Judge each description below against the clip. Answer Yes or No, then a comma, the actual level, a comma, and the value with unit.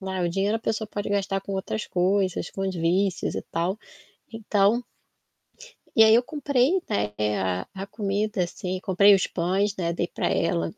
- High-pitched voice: Yes, high, 195 Hz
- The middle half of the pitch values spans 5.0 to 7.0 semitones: No, narrow, 2.6 semitones